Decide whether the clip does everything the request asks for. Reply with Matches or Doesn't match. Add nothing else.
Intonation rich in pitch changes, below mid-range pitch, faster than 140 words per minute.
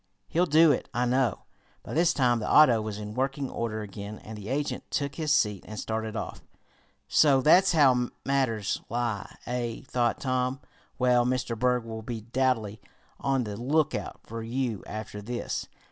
Doesn't match